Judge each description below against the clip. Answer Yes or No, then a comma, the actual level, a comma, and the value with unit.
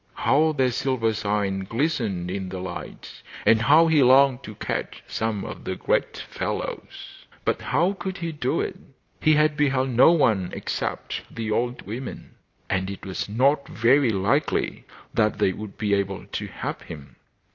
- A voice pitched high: No, low, 115 Hz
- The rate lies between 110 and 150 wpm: No, average, 165 wpm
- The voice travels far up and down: Yes, wide, 5.9 semitones